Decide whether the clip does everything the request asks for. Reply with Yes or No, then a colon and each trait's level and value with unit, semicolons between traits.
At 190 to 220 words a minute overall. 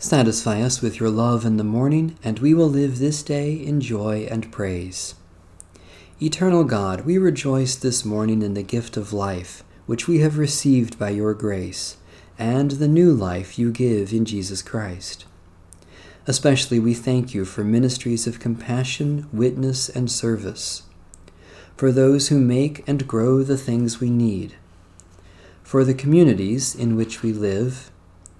No: average, 155 wpm